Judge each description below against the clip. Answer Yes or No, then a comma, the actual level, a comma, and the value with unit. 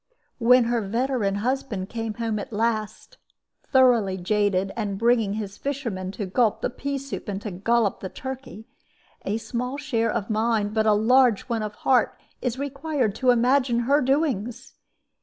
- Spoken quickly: No, average, 160 wpm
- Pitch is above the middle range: Yes, high, 230 Hz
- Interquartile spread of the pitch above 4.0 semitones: No, average, 3.5 semitones